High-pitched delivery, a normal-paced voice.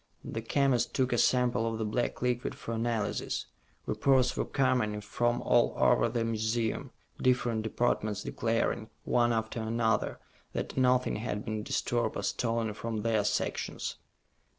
No: low, 115 Hz; average, 150 wpm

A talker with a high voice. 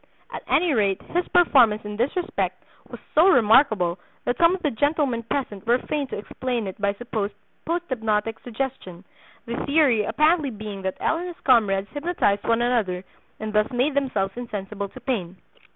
Yes: high, 235 Hz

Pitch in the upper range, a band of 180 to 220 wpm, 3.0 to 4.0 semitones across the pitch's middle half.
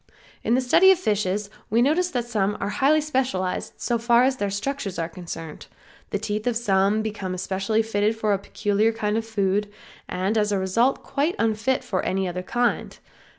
Yes: high, 215 Hz; average, 190 wpm; average, 3.6 semitones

